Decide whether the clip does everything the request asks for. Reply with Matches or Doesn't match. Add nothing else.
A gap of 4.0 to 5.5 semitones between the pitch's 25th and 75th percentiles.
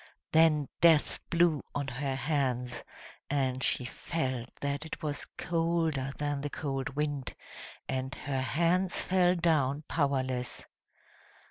Doesn't match